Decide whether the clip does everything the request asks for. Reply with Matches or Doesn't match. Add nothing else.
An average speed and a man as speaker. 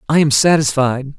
Matches